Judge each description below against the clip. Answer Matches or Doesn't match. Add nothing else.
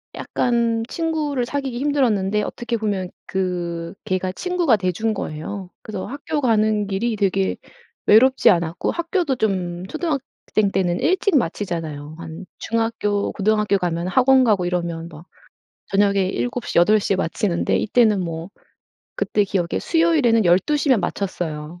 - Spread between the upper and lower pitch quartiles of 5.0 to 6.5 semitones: Matches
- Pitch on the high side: Matches